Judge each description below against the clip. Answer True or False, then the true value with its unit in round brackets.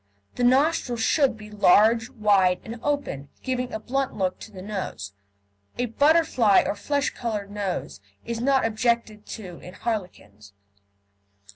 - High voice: True (220 Hz)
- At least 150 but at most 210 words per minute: False (140 wpm)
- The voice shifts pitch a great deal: False (4.0 semitones)